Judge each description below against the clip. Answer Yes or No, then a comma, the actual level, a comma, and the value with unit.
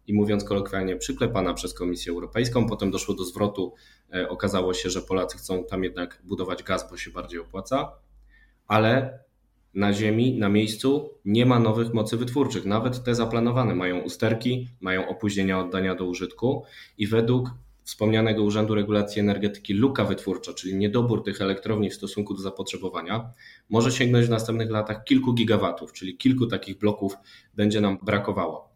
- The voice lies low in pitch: Yes, low, 105 Hz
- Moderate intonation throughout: Yes, average, 3.5 semitones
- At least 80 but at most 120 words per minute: No, average, 155 wpm